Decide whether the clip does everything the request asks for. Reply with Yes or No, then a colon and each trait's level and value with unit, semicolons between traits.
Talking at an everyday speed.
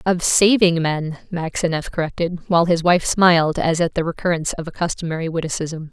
Yes: average, 170 wpm